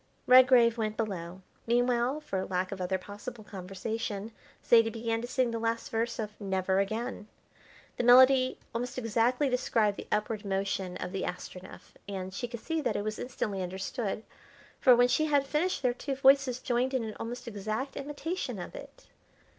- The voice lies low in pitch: No, high, 230 Hz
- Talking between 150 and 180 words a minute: Yes, average, 170 wpm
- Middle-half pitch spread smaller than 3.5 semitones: No, average, 4.1 semitones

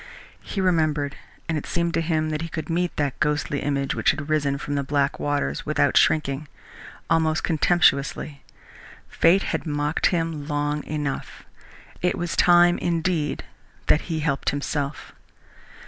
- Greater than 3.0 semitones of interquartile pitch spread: No, narrow, 2.4 semitones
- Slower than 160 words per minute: Yes, average, 145 wpm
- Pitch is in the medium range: Yes, medium, 155 Hz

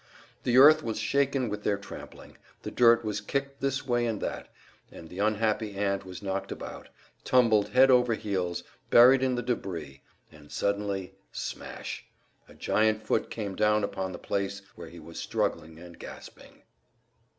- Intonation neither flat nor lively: Yes, average, 4.0 semitones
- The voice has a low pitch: Yes, low, 105 Hz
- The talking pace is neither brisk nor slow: Yes, average, 160 wpm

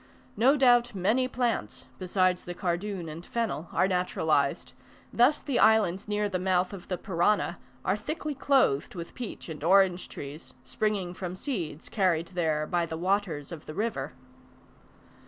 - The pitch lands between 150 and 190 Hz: Yes, medium, 185 Hz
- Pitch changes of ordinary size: Yes, average, 4.1 semitones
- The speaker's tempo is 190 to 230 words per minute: No, average, 155 wpm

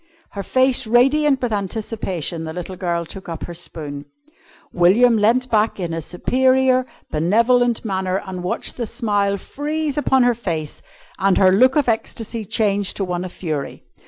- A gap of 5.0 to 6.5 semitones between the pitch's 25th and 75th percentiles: Yes, wide, 5.5 semitones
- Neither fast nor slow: Yes, average, 160 wpm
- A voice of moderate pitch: No, high, 205 Hz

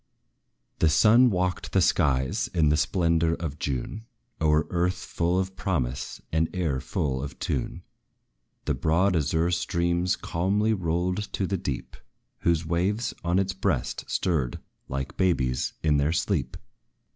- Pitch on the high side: No, very low, 85 Hz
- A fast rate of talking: No, average, 140 wpm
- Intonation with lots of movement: No, average, 3.7 semitones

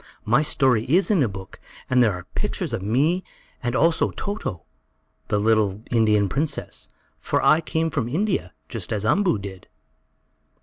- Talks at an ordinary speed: Yes, average, 160 wpm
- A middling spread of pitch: No, wide, 7.5 semitones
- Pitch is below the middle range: Yes, low, 120 Hz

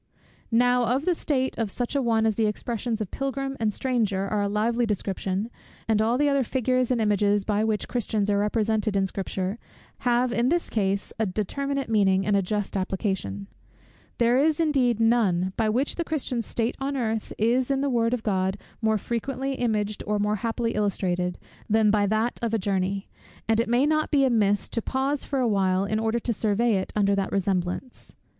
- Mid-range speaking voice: No, high, 220 Hz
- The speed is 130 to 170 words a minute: No, average, 195 wpm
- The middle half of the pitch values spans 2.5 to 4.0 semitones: Yes, average, 3.5 semitones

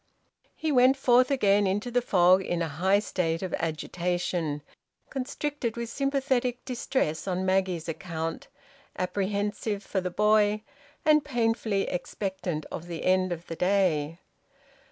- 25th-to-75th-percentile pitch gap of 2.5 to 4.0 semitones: No, average, 5.3 semitones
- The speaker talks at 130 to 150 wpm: Yes, slow, 135 wpm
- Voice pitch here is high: Yes, high, 195 Hz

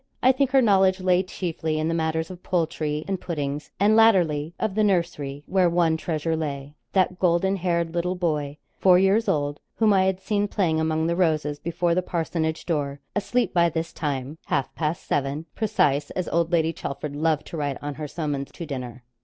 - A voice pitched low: No, medium, 165 Hz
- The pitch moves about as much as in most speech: Yes, average, 3.5 semitones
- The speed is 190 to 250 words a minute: Yes, average, 195 wpm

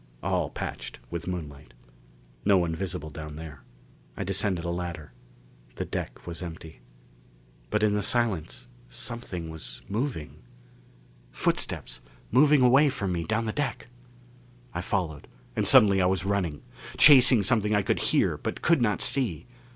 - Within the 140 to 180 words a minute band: Yes, average, 145 wpm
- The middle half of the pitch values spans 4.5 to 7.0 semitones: Yes, average, 5.1 semitones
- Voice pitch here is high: No, very low, 95 Hz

